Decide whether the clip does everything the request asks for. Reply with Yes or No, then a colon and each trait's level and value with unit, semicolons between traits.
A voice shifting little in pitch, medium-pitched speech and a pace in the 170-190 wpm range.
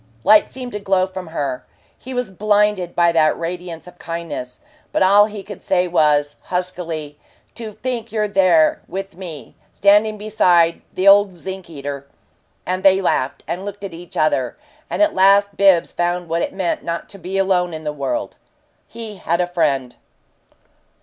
No: average, 3.3 semitones; medium, 180 Hz; average, 175 wpm